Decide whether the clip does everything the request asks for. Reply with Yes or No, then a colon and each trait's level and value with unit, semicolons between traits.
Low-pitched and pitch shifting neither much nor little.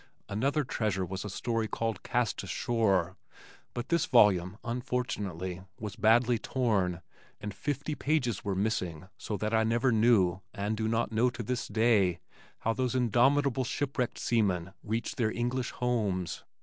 Yes: low, 115 Hz; average, 3.8 semitones